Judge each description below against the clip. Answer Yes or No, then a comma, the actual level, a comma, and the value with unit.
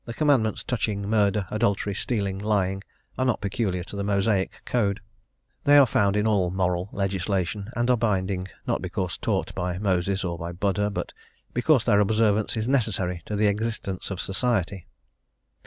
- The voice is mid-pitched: No, low, 100 Hz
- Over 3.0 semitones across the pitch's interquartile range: No, average, 2.7 semitones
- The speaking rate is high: No, average, 165 wpm